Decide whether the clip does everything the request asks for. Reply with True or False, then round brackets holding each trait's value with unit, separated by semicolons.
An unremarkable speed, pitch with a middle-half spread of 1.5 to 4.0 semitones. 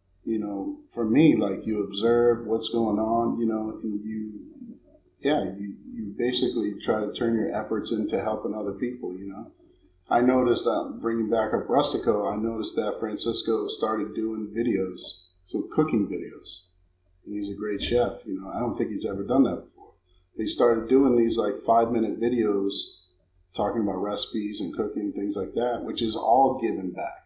True (180 wpm; 2.7 semitones)